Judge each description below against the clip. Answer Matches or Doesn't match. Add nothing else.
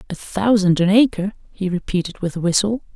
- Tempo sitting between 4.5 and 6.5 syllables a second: Matches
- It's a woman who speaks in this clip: Matches